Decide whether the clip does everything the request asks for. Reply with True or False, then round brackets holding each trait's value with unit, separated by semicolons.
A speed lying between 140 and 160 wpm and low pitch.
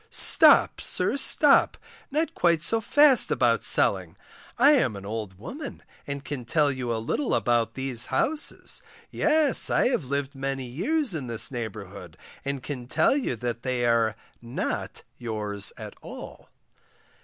True (150 wpm; 130 Hz)